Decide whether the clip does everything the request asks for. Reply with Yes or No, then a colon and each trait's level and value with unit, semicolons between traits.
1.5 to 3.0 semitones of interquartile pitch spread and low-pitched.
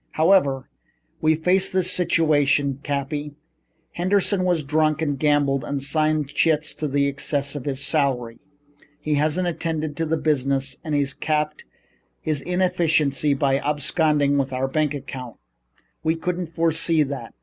No: narrow, 2.5 semitones; medium, 150 Hz